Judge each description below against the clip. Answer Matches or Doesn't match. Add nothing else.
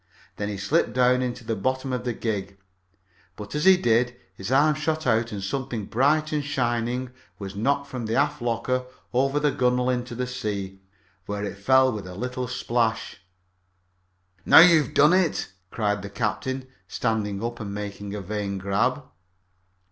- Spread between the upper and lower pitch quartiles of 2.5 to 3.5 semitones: Doesn't match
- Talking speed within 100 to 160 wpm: Doesn't match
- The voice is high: Doesn't match